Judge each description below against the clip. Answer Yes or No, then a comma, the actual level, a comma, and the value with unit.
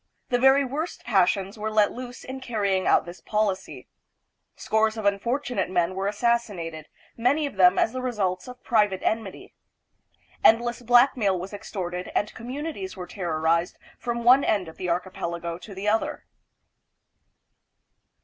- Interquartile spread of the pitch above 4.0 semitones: Yes, average, 4.6 semitones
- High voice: Yes, high, 210 Hz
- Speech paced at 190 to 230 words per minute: No, average, 150 wpm